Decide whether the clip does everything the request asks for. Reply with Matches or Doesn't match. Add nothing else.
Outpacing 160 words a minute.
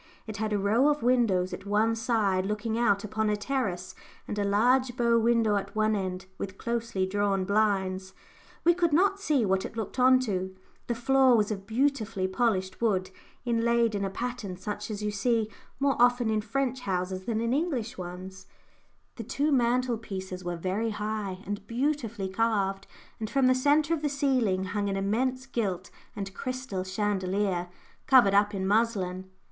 Matches